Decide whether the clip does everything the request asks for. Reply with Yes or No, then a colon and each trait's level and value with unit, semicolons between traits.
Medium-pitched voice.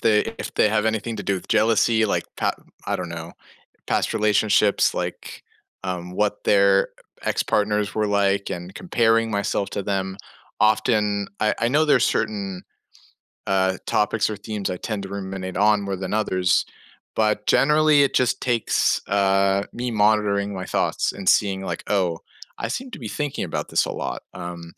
No: low, 105 Hz